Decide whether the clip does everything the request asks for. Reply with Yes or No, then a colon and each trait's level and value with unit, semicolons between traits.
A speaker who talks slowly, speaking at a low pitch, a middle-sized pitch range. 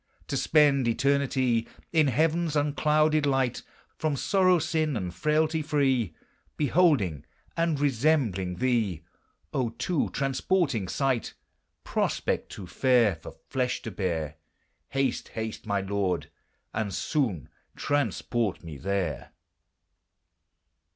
No: slow, 105 wpm; low, 130 Hz; wide, 6.9 semitones